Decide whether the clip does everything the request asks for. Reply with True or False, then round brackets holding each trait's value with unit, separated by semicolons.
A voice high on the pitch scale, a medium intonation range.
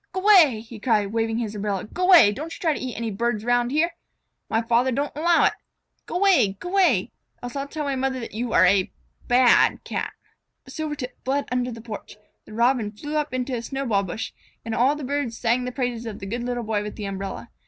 True (245 Hz; 4.3 semitones)